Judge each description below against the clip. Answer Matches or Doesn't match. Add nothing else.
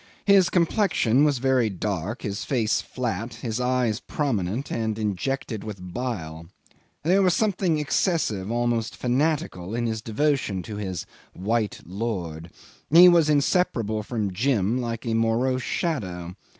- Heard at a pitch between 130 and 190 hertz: Doesn't match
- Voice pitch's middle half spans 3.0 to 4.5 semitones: Doesn't match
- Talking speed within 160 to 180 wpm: Doesn't match